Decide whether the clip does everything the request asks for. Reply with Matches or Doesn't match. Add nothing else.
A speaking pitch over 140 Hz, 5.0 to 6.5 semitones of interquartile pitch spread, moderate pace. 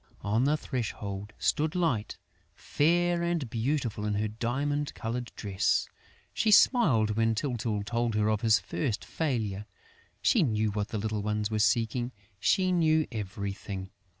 Doesn't match